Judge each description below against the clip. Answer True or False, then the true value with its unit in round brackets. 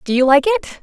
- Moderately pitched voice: False (280 Hz)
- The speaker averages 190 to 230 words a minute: False (290 wpm)